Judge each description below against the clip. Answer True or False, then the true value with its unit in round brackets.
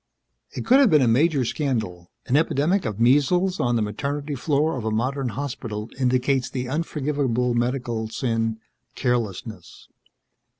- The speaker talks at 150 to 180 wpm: False (140 wpm)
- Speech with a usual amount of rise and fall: True (4.1 semitones)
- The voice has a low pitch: True (130 Hz)